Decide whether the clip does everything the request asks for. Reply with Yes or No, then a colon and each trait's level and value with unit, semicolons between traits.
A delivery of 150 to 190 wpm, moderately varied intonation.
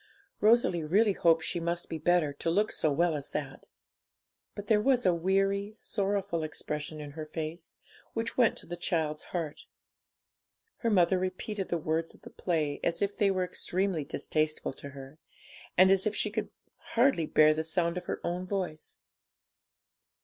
Yes: average, 170 wpm; average, 4.0 semitones